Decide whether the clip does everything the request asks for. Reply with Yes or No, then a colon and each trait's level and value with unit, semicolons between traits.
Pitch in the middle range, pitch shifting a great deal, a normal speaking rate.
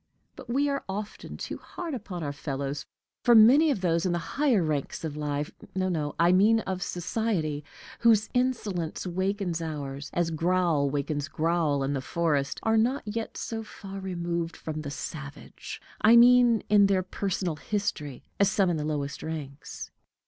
Yes: medium, 175 Hz; wide, 5.8 semitones; average, 170 wpm